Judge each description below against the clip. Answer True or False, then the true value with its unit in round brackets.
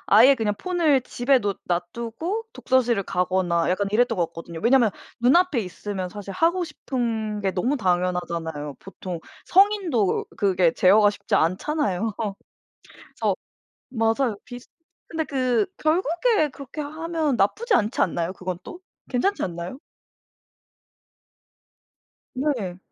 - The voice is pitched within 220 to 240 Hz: True (225 Hz)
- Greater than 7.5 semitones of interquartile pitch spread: True (7.9 semitones)